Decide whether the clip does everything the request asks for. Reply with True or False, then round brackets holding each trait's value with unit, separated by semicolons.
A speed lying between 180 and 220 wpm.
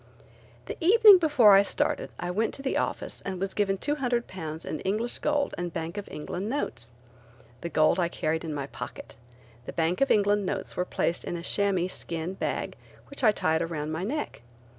True (190 wpm)